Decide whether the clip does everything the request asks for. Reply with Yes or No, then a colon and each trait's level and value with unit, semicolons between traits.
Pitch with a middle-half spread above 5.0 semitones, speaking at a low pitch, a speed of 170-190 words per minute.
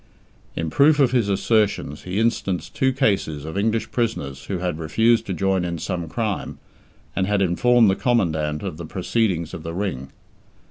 Yes: wide, 5.4 semitones; very low, 95 Hz; average, 175 wpm